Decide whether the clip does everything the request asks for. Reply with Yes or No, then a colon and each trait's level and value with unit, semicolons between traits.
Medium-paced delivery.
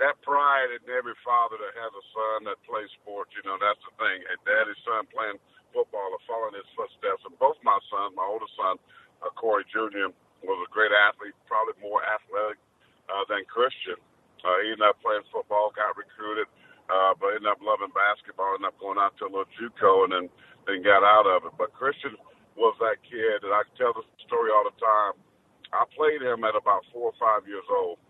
No: fast, 210 wpm